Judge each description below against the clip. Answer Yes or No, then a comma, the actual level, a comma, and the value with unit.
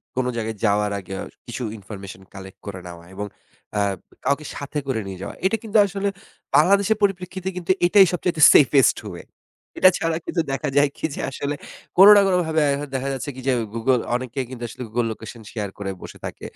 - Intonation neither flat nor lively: No, wide, 8.5 semitones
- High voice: No, low, 130 Hz